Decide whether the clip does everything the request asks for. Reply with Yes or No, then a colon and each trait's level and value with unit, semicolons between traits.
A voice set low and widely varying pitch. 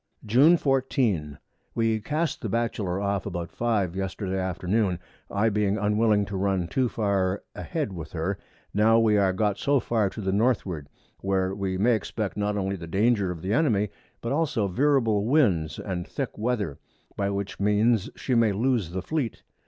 No: low, 105 Hz; average, 3.4 semitones